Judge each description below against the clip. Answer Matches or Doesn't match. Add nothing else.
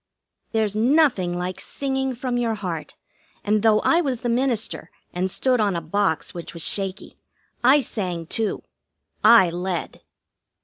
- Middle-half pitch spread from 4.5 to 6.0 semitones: Matches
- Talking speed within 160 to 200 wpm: Doesn't match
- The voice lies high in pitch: Matches